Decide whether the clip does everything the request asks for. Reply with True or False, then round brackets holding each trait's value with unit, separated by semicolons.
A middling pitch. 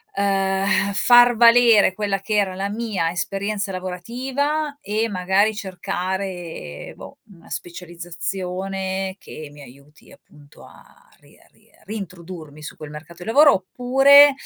False (195 Hz)